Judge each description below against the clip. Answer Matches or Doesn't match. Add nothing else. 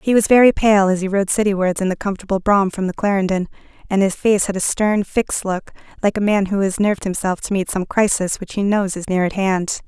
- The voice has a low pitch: Doesn't match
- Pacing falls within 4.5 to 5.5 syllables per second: Doesn't match